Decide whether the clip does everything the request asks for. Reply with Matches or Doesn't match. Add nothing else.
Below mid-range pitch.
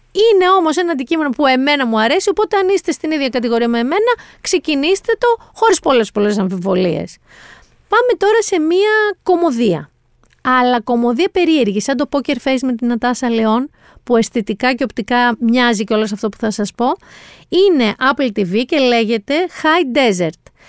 Doesn't match